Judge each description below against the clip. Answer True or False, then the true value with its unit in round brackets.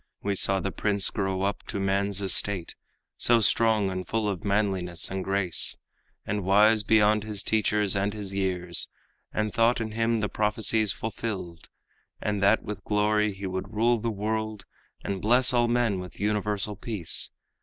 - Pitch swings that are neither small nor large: False (2.0 semitones)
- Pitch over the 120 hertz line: False (105 Hz)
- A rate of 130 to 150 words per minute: False (165 wpm)